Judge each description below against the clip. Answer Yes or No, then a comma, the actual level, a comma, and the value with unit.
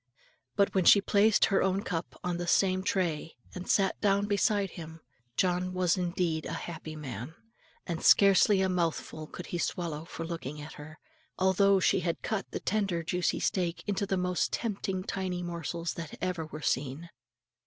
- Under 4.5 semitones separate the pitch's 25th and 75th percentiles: Yes, average, 2.8 semitones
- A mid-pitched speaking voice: Yes, medium, 180 Hz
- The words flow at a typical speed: Yes, average, 175 wpm